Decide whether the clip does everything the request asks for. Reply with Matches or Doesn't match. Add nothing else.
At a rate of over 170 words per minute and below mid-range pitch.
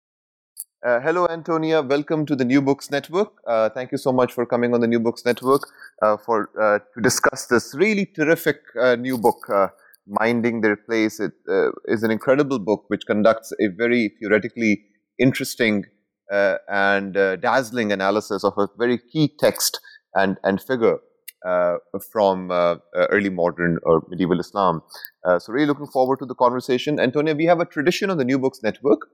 Matches